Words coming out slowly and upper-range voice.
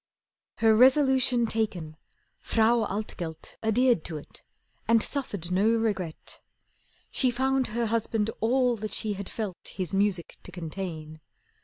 Yes: slow, 130 wpm; high, 220 Hz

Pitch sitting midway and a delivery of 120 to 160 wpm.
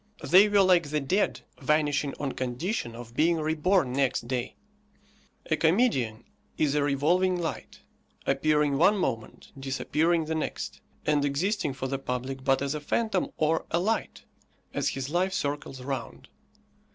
Yes: medium, 150 Hz; average, 150 wpm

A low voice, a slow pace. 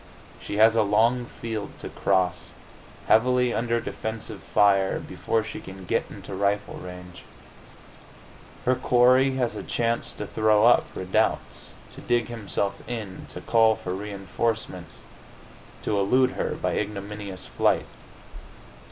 Yes: low, 110 Hz; slow, 130 wpm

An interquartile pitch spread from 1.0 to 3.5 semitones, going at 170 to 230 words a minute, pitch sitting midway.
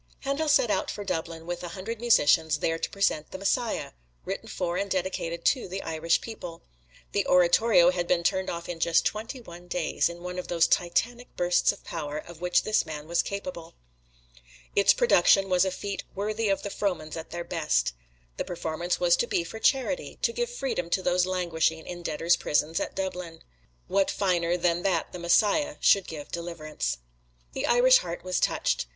Yes: average, 3.2 semitones; average, 190 wpm; medium, 180 Hz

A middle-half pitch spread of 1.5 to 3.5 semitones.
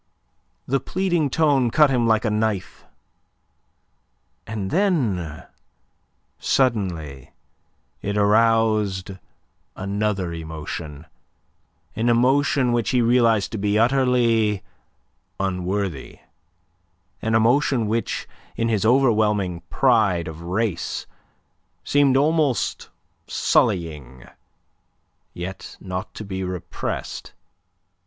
No: average, 4.8 semitones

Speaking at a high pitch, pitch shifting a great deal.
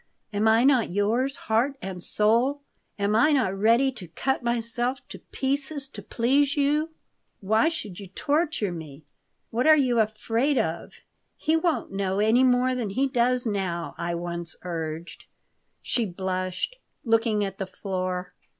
Yes: high, 225 Hz; wide, 5.9 semitones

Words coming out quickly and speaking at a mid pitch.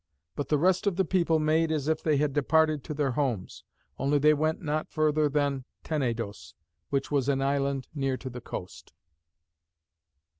No: average, 175 wpm; medium, 145 Hz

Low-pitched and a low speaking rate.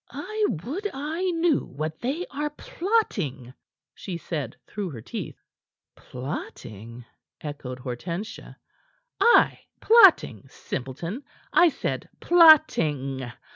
No: medium, 175 Hz; slow, 95 wpm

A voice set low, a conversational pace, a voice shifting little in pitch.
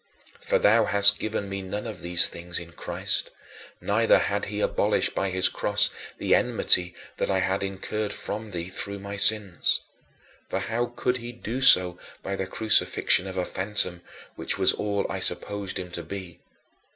Yes: low, 100 Hz; average, 175 wpm; narrow, 2.3 semitones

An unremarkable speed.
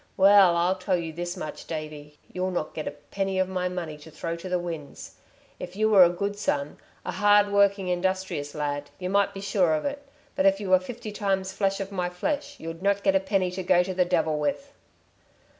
No: fast, 220 wpm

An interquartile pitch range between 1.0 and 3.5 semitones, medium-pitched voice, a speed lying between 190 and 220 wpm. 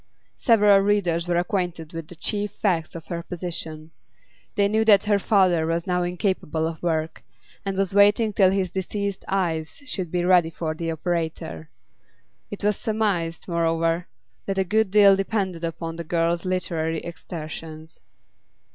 No: average, 3.1 semitones; medium, 175 Hz; average, 155 wpm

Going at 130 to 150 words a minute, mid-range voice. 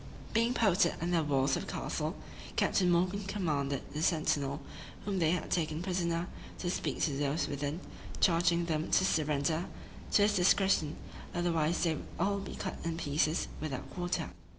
No: average, 165 wpm; medium, 170 Hz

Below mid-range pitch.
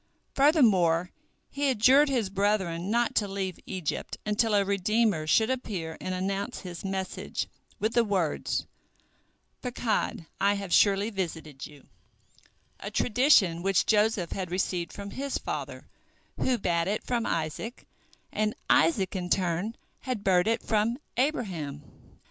No: high, 195 Hz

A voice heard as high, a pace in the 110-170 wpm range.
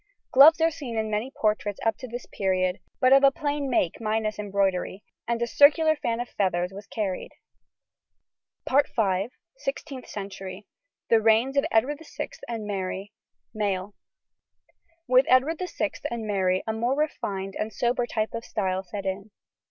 Yes: high, 220 Hz; average, 150 wpm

